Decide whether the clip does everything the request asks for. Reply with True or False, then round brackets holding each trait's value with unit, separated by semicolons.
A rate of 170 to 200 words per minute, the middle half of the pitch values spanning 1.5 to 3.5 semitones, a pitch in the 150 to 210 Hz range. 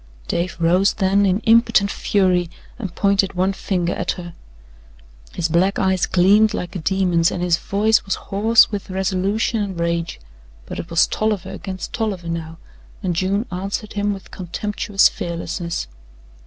False (155 wpm; 2.7 semitones; 190 Hz)